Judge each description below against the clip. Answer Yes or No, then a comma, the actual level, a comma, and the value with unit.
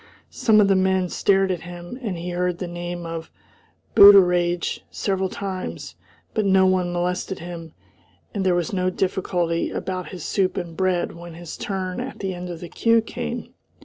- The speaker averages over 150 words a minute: Yes, average, 180 wpm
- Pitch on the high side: No, medium, 180 Hz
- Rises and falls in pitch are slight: Yes, narrow, 1.7 semitones